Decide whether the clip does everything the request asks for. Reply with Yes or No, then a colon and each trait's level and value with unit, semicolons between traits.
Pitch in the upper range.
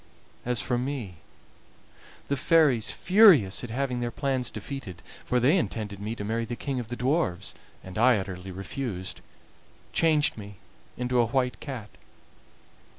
No: low, 120 Hz